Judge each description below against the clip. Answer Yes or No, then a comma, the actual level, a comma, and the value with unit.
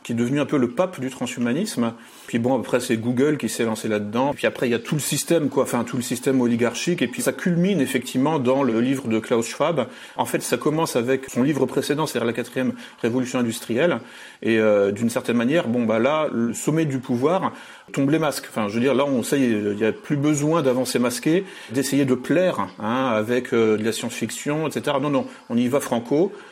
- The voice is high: No, low, 125 Hz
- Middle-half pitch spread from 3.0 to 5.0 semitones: Yes, average, 3.8 semitones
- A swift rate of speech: Yes, fast, 230 wpm